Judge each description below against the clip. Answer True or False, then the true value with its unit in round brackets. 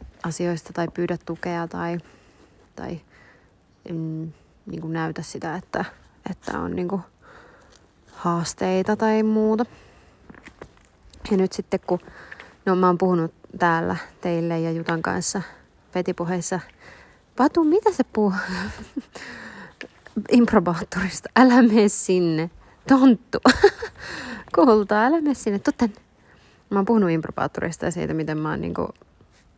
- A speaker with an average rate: True (115 wpm)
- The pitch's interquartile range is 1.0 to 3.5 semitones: False (4.5 semitones)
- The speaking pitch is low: False (185 Hz)